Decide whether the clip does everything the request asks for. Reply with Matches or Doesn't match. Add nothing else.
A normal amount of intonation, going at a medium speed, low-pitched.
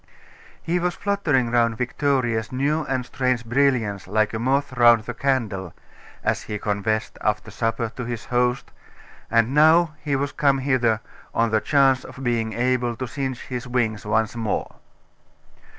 Matches